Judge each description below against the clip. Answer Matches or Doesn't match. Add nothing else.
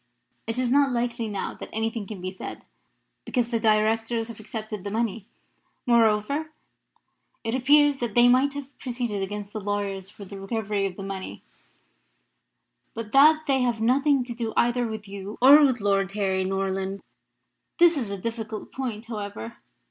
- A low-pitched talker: Doesn't match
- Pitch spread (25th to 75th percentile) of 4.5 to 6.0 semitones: Doesn't match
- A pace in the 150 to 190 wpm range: Matches